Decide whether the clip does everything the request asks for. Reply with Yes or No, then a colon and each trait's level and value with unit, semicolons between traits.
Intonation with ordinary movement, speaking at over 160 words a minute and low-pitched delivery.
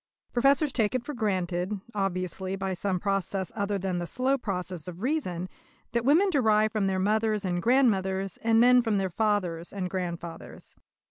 No: average, 3.8 semitones; average, 170 wpm; high, 195 Hz